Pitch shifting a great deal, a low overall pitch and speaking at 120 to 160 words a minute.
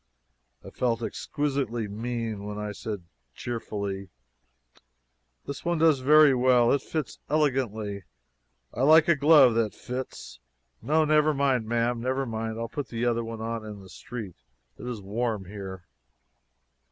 No: average, 4.2 semitones; low, 120 Hz; average, 140 wpm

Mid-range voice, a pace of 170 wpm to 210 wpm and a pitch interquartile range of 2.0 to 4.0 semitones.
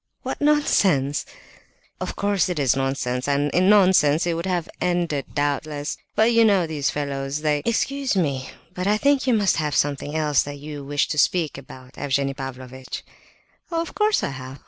No: medium, 150 Hz; average, 175 wpm; wide, 5.4 semitones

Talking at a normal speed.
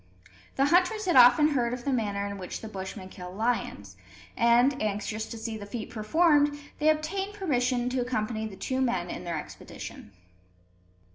Yes: average, 170 wpm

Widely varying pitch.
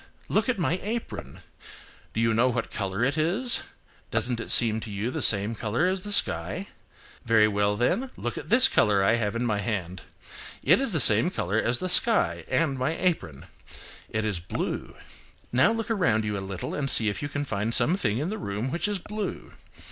Yes: wide, 9.0 semitones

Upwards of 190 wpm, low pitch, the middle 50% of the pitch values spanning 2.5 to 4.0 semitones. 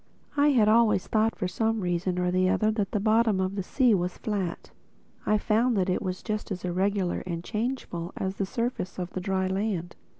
No: average, 200 wpm; high, 195 Hz; average, 3.2 semitones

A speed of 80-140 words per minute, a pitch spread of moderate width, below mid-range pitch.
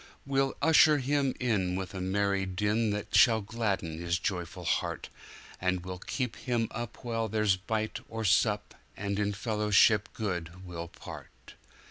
Yes: slow, 135 wpm; average, 3.5 semitones; low, 105 Hz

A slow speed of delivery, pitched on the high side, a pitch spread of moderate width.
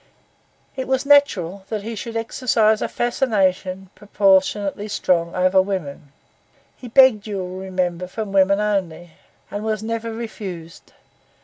Yes: slow, 130 wpm; high, 200 Hz; average, 3.3 semitones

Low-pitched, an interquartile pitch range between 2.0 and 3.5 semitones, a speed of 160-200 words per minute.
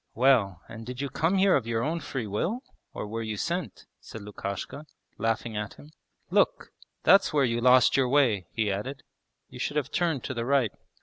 No: low, 125 Hz; average, 4.6 semitones; average, 195 wpm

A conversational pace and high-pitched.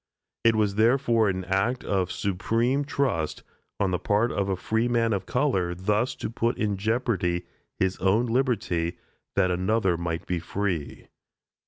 No: average, 150 wpm; low, 100 Hz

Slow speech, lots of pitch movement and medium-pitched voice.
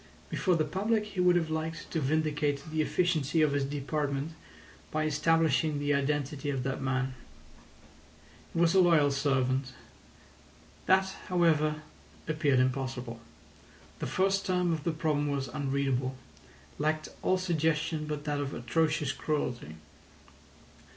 No: slow, 130 wpm; average, 2.9 semitones; medium, 150 Hz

